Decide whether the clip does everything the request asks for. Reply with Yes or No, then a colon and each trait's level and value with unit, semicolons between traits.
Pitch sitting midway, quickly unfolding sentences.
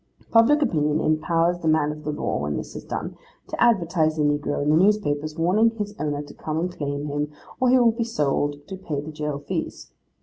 Yes: medium, 155 Hz; fast, 210 wpm